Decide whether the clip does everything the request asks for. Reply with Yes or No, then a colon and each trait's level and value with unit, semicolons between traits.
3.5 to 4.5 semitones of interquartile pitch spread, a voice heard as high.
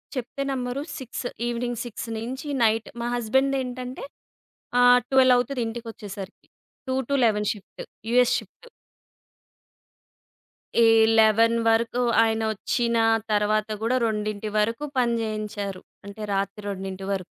No: average, 2.8 semitones; high, 230 Hz